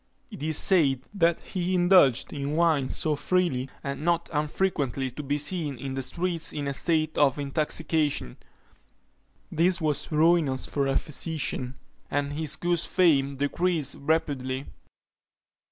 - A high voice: No, medium, 150 Hz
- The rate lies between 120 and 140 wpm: Yes, slow, 135 wpm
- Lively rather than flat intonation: No, average, 3.4 semitones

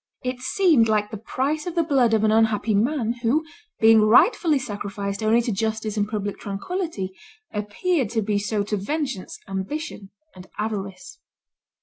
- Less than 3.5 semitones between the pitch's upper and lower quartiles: No, average, 4.6 semitones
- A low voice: No, high, 220 Hz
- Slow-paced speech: No, average, 155 wpm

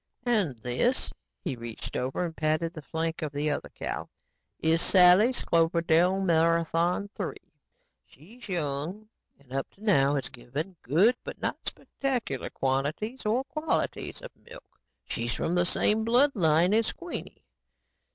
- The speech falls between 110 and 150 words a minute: Yes, average, 140 wpm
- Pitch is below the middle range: No, medium, 170 Hz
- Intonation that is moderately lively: No, wide, 6.4 semitones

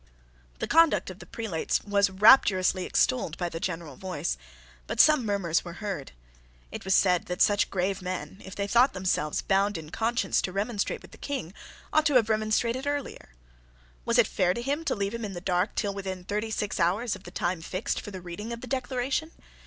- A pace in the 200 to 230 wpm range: Yes, fast, 205 wpm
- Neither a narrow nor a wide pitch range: Yes, average, 4.2 semitones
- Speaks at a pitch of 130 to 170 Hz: No, high, 200 Hz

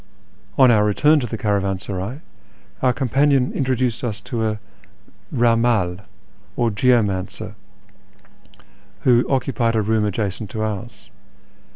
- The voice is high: No, low, 115 Hz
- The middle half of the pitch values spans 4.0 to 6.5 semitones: No, average, 3.4 semitones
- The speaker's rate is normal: No, slow, 110 wpm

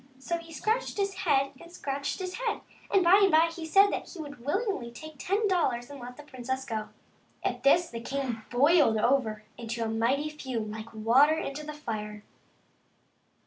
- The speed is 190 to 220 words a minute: Yes, average, 195 wpm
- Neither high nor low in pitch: No, very high, 280 Hz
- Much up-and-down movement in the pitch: Yes, wide, 6.2 semitones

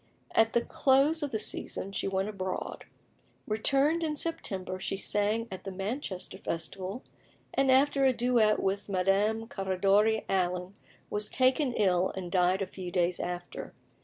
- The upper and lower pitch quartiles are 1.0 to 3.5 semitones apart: No, average, 4.8 semitones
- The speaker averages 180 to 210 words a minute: No, average, 150 wpm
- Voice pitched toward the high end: Yes, high, 200 Hz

